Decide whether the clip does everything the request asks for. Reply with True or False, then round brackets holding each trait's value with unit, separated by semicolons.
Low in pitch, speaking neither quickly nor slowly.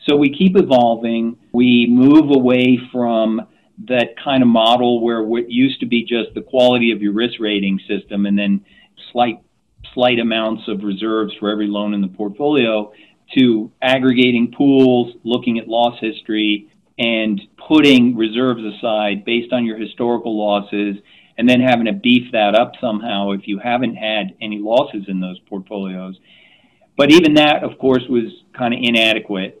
True (115 Hz; 160 wpm)